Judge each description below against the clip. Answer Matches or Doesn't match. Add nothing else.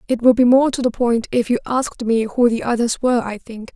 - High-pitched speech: Matches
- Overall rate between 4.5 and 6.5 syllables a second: Matches